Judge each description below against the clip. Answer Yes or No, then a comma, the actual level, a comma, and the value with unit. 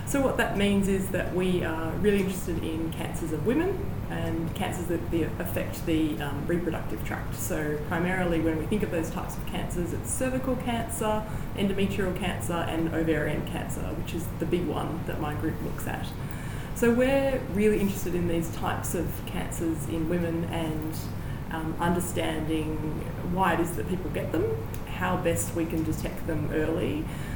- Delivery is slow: No, average, 170 wpm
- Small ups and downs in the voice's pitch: No, average, 3.6 semitones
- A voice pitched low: No, medium, 165 Hz